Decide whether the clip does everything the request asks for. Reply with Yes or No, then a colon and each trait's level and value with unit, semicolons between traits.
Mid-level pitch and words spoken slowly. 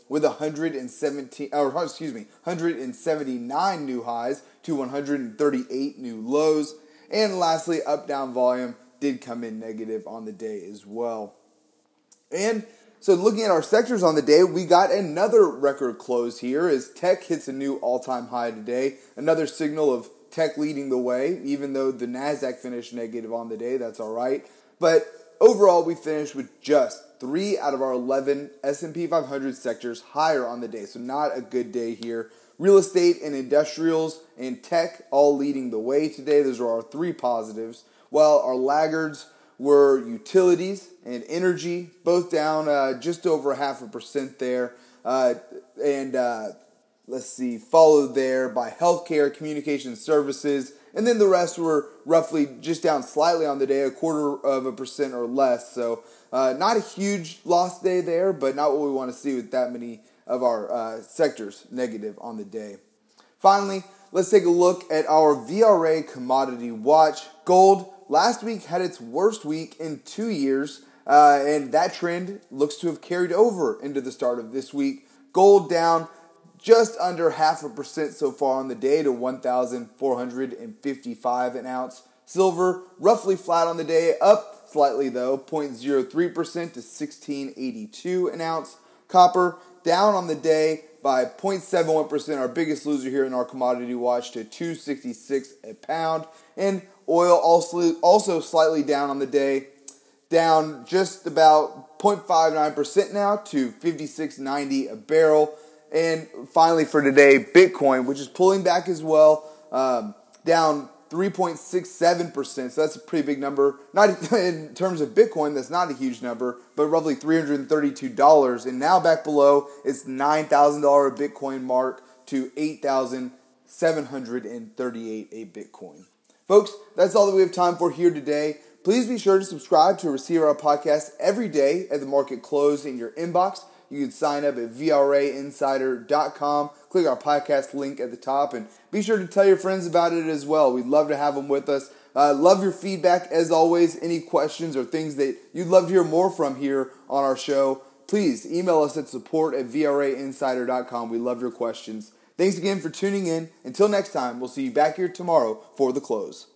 No: medium, 150 Hz; average, 165 wpm